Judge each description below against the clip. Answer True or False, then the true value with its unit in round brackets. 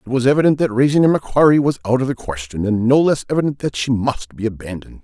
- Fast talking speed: True (250 wpm)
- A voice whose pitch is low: True (125 Hz)